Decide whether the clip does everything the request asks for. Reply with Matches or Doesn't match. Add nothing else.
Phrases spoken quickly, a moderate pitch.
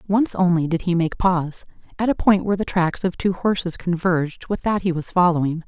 Matches